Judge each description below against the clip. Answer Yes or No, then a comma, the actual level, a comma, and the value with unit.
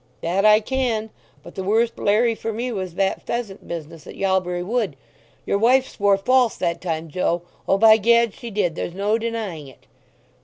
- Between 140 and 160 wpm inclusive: No, average, 170 wpm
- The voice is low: No, high, 205 Hz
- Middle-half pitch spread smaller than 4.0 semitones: No, average, 4.3 semitones